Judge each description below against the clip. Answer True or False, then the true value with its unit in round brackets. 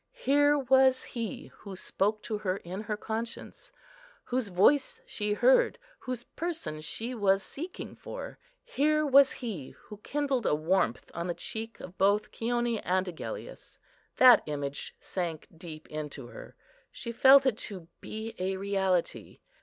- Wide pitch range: True (6.0 semitones)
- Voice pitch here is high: True (215 Hz)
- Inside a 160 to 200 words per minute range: False (145 wpm)